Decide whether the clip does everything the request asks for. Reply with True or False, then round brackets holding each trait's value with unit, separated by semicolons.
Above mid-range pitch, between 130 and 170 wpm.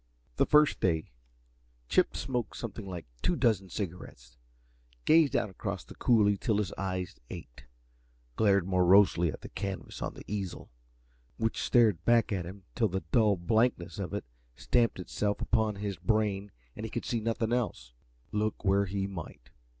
False (100 Hz; 160 wpm)